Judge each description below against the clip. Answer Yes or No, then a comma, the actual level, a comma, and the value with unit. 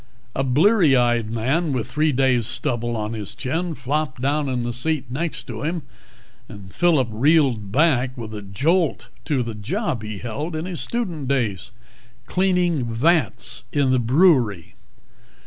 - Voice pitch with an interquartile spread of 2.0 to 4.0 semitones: No, average, 5.3 semitones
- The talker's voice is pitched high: No, low, 130 Hz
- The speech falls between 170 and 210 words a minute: No, average, 160 wpm